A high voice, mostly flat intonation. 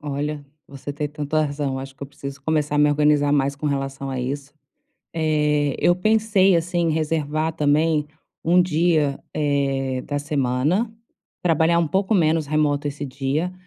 No: medium, 150 Hz; narrow, 2.3 semitones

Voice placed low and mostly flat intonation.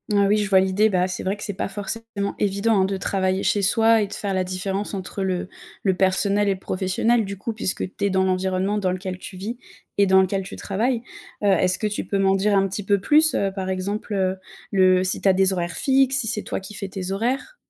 No: high, 195 Hz; narrow, 1.7 semitones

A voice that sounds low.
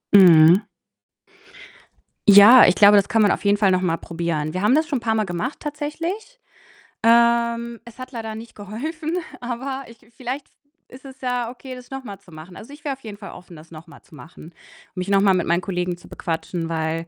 No: high, 215 Hz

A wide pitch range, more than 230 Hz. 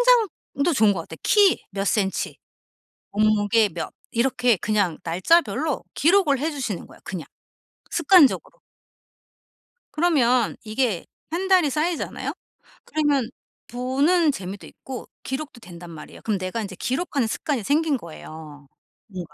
Yes: wide, 7.6 semitones; high, 245 Hz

